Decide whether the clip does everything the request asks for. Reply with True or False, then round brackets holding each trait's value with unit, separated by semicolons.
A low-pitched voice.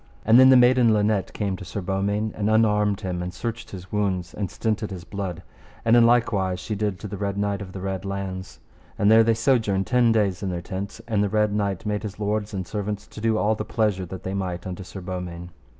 True (100 Hz)